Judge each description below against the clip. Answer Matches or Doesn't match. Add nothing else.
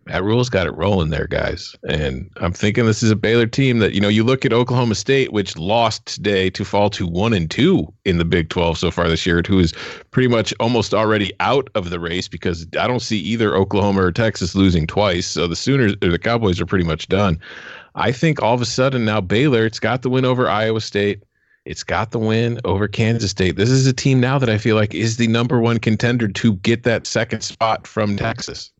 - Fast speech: Matches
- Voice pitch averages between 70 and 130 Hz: Matches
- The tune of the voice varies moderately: Matches